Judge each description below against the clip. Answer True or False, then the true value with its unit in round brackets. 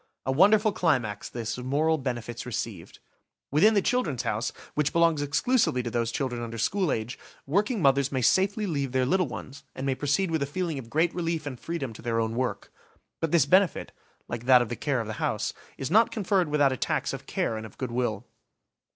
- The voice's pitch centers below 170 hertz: True (140 Hz)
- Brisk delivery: True (210 wpm)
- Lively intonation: True (5.9 semitones)